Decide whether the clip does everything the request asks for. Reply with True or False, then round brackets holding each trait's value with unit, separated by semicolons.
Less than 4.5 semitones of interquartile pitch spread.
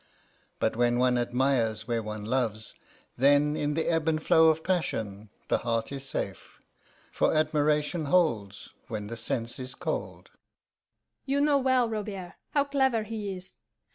False (5.1 semitones)